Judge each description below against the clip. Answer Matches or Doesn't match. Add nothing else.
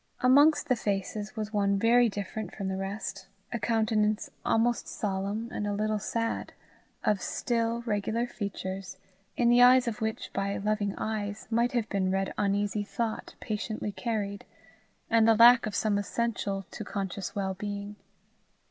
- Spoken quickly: Doesn't match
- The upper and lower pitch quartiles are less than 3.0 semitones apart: Matches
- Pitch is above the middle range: Matches